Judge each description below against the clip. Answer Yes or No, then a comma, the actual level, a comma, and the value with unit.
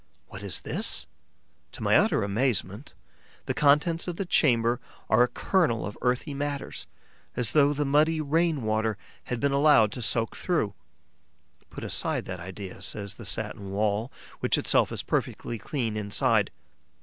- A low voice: Yes, low, 120 Hz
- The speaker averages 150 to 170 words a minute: Yes, average, 155 wpm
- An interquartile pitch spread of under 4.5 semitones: No, wide, 5.6 semitones